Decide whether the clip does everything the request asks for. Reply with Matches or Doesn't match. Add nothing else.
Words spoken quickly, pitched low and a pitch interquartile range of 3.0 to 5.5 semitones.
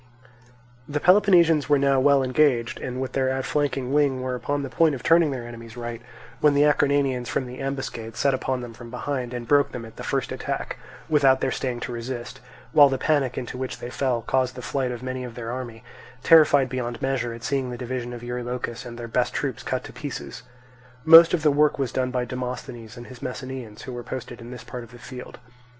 Doesn't match